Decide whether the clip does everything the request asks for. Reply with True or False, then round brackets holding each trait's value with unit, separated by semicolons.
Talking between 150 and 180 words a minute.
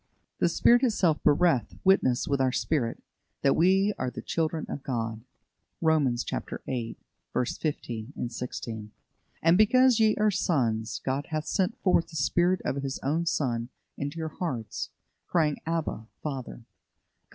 False (140 wpm)